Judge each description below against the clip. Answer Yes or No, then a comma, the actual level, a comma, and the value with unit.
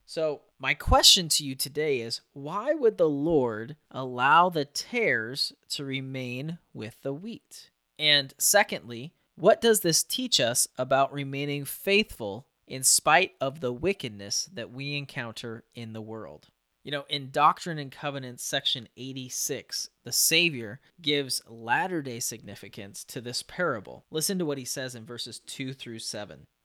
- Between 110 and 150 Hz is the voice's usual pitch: Yes, low, 135 Hz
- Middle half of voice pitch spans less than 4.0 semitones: No, average, 4.5 semitones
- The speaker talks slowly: No, average, 150 wpm